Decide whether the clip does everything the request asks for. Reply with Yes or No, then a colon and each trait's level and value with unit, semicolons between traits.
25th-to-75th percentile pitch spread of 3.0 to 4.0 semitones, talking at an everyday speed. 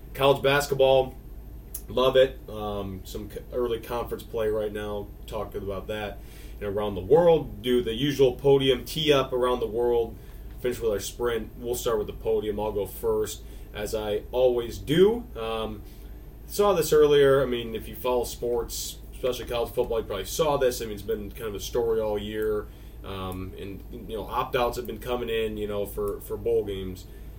No: average, 4.8 semitones; average, 190 wpm